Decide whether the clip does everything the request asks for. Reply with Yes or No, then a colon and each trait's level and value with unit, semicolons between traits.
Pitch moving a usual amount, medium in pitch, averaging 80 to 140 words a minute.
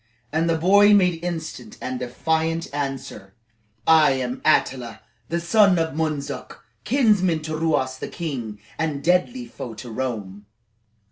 Yes: average, 4.8 semitones; medium, 155 Hz; slow, 135 wpm